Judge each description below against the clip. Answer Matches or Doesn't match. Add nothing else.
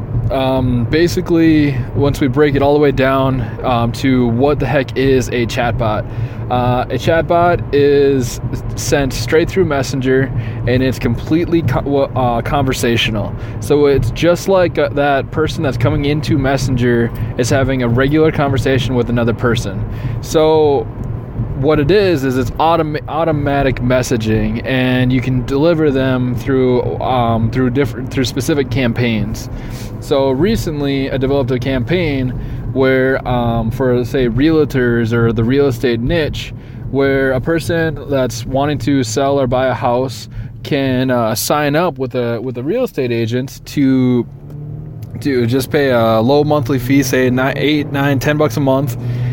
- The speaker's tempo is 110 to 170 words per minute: Matches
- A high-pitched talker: Doesn't match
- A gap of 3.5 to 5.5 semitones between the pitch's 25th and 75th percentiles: Doesn't match